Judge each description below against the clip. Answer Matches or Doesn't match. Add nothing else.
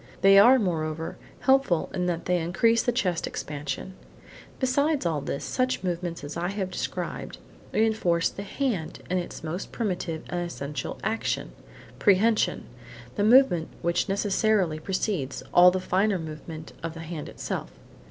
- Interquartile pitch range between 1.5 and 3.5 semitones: Doesn't match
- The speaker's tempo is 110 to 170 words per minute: Matches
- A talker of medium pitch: Matches